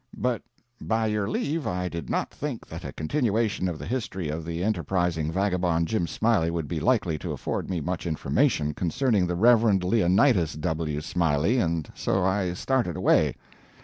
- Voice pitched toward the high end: No, very low, 90 Hz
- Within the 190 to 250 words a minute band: No, average, 170 wpm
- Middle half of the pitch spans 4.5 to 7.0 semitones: Yes, average, 5.0 semitones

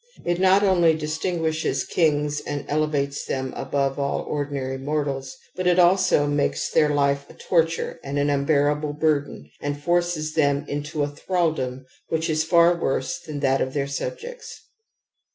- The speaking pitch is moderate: Yes, medium, 150 Hz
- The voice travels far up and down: No, average, 2.7 semitones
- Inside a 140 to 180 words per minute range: Yes, average, 155 wpm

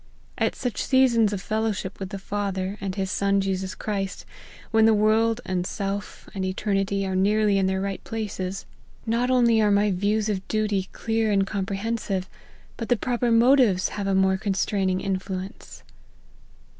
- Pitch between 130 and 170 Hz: No, high, 200 Hz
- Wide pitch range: No, narrow, 2.4 semitones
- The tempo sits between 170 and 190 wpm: Yes, average, 180 wpm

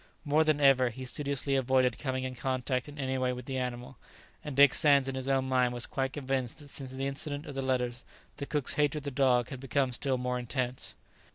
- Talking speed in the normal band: No, fast, 225 wpm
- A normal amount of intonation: No, narrow, 1.8 semitones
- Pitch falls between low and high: No, low, 130 Hz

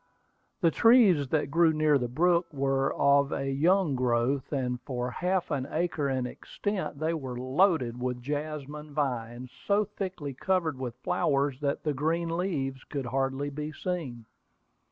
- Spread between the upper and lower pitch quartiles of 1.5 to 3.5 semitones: No, average, 4.0 semitones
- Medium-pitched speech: Yes, medium, 145 Hz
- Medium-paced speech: Yes, average, 155 wpm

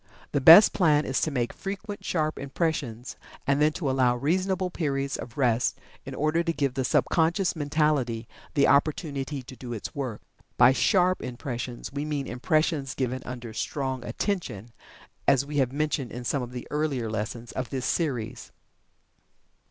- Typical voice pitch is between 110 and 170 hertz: Yes, medium, 140 Hz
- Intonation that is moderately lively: Yes, average, 3.8 semitones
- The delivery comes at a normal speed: Yes, average, 165 wpm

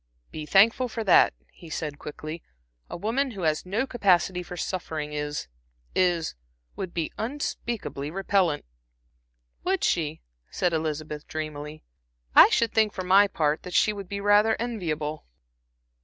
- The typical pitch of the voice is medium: Yes, medium, 180 Hz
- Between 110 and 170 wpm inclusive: Yes, average, 140 wpm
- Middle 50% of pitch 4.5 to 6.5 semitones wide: Yes, average, 5.1 semitones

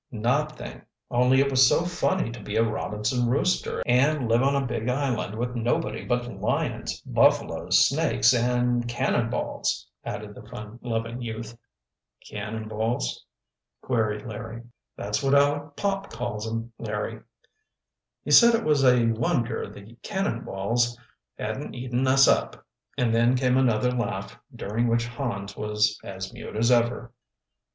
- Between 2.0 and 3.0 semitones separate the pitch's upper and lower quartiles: Yes, narrow, 2.6 semitones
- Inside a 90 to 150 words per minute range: Yes, average, 140 wpm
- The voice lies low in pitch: Yes, low, 120 Hz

